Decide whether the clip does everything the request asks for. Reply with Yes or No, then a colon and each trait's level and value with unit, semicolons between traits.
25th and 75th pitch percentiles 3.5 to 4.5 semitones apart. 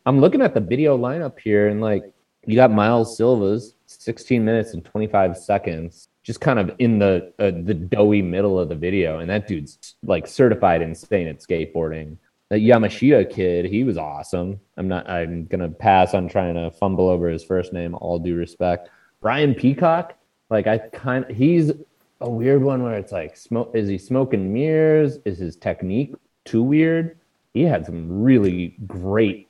No: average, 5.2 semitones